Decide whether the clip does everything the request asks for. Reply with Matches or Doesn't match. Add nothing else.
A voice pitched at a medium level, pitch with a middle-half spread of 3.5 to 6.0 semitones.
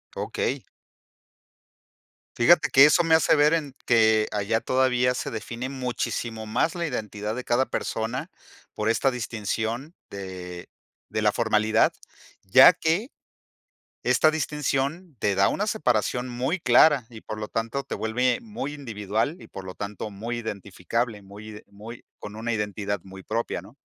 Doesn't match